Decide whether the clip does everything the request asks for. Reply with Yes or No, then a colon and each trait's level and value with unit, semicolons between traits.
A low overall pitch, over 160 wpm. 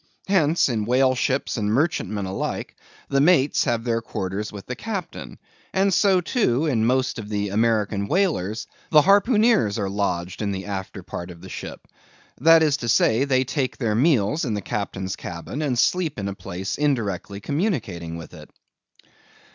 Yes: low, 115 Hz; average, 170 wpm